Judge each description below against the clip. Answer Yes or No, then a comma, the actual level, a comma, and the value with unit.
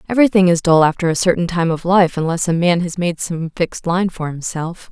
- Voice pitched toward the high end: No, medium, 175 Hz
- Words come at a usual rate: No, fast, 230 wpm